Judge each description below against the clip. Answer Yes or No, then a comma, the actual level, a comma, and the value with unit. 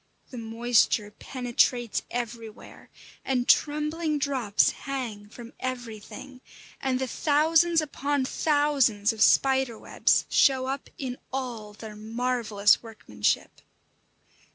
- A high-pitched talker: Yes, very high, 250 Hz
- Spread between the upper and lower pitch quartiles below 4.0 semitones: Yes, average, 3.6 semitones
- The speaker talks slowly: Yes, slow, 105 wpm